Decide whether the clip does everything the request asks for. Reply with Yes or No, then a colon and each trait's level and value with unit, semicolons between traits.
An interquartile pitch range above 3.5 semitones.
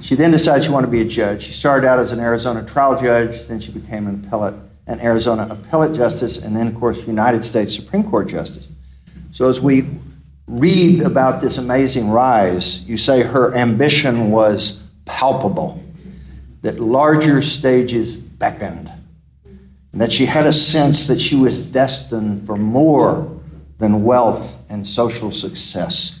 Yes: average, 4.3 semitones